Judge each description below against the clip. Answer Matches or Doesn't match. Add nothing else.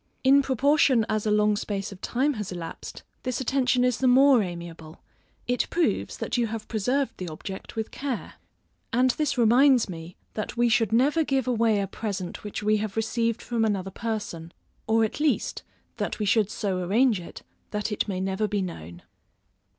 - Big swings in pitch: Doesn't match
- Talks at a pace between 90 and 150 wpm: Doesn't match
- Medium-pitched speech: Doesn't match